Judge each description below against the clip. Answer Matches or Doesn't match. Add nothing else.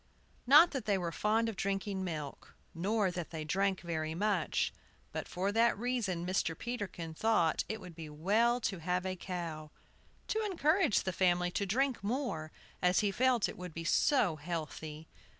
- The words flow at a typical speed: Matches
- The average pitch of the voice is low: Doesn't match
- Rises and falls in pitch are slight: Doesn't match